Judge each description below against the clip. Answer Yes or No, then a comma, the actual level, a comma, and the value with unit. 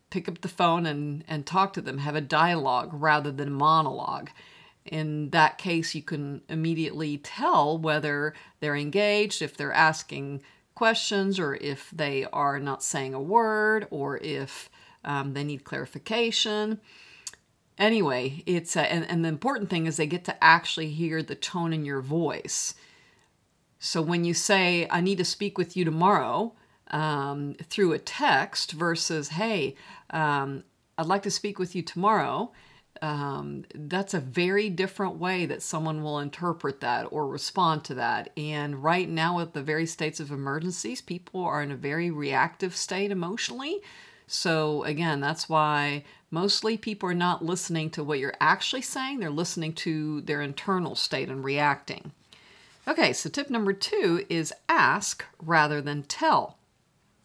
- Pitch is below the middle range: No, medium, 165 Hz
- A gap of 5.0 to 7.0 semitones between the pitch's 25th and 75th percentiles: No, average, 4.3 semitones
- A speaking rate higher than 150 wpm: Yes, average, 160 wpm